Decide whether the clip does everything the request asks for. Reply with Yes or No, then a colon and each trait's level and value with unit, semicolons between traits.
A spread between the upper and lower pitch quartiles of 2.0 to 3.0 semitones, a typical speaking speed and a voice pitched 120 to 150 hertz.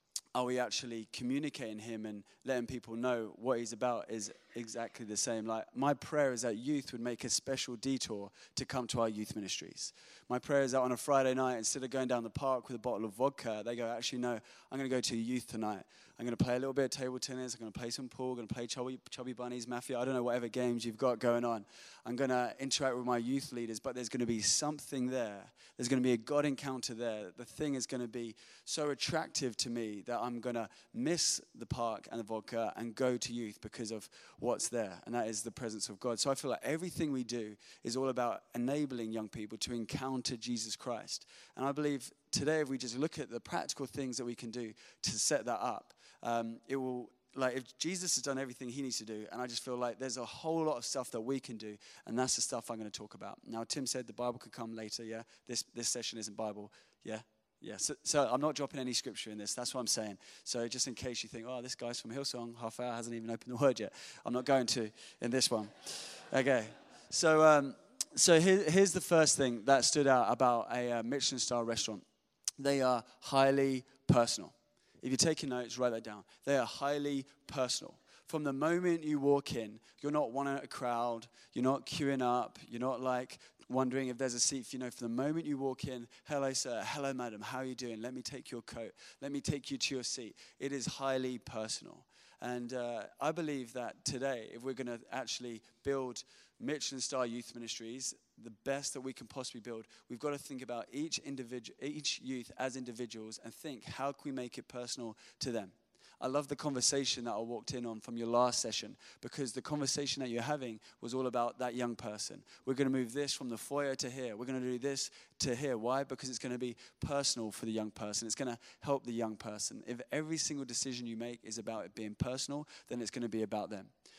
No: narrow, 2.6 semitones; fast, 240 wpm; low, 125 Hz